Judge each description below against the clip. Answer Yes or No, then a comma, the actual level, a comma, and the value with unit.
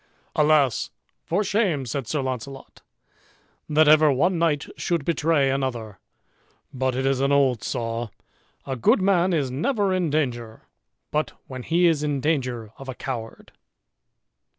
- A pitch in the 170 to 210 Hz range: No, medium, 140 Hz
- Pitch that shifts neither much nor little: Yes, average, 4.0 semitones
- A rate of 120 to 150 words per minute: Yes, average, 145 wpm